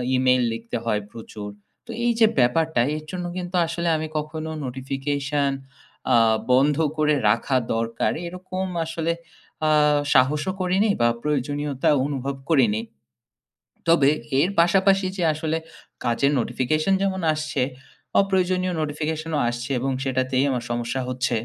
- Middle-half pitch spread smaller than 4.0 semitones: No, average, 4.6 semitones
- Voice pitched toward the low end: No, medium, 145 Hz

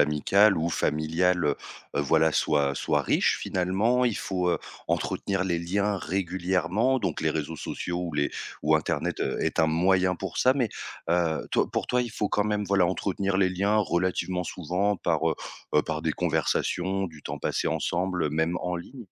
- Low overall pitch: Yes, very low, 90 Hz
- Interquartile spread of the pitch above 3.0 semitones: Yes, average, 3.4 semitones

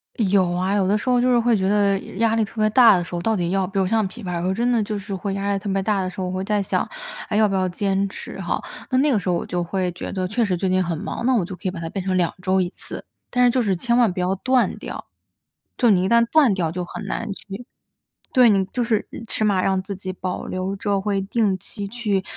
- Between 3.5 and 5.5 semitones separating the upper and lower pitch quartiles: No, average, 3.0 semitones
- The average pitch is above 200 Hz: No, high, 195 Hz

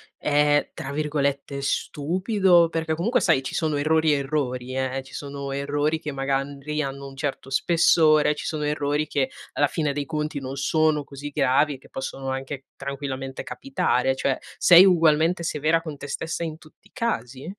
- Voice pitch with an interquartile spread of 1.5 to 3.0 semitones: Yes, narrow, 2.4 semitones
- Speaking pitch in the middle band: Yes, medium, 145 Hz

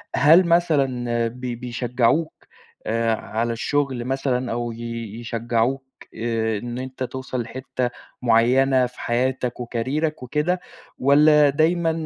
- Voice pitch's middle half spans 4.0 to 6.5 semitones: No, average, 3.1 semitones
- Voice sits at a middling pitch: No, low, 125 Hz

